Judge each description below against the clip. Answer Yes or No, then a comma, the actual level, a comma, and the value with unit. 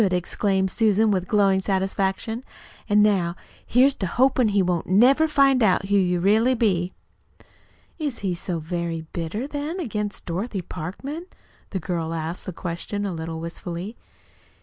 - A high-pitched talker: Yes, high, 195 Hz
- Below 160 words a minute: Yes, average, 150 wpm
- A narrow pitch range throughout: No, average, 4.3 semitones